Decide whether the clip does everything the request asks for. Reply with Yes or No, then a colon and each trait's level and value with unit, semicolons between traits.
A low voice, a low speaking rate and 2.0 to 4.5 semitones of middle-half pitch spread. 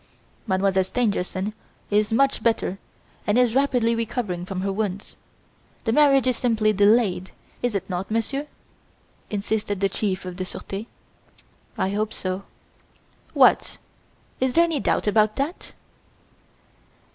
No: high, 215 Hz; slow, 130 wpm; average, 3.9 semitones